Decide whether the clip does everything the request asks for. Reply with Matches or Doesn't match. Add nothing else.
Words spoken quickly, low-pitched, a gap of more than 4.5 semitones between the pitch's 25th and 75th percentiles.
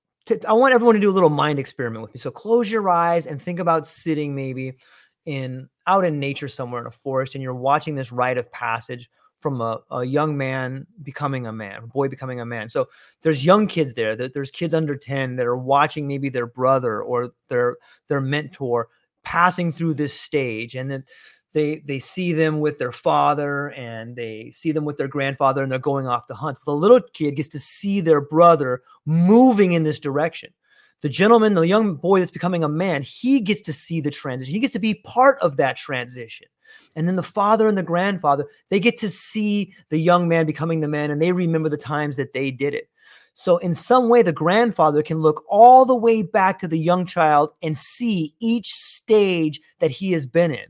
Doesn't match